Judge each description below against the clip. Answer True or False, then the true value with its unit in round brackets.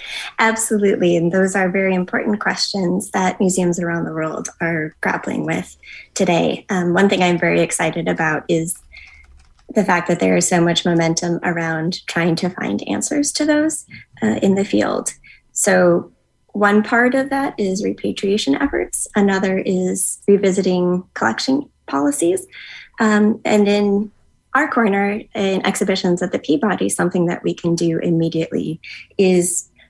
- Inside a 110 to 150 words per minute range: True (145 wpm)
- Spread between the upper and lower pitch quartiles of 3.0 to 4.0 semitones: True (3.5 semitones)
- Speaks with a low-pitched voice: False (190 Hz)